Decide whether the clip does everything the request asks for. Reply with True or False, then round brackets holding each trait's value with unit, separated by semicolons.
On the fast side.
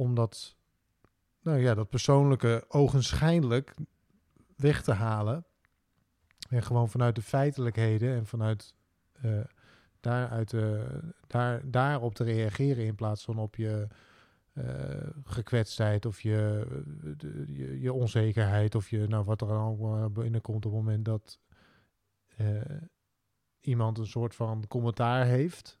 False (130 wpm)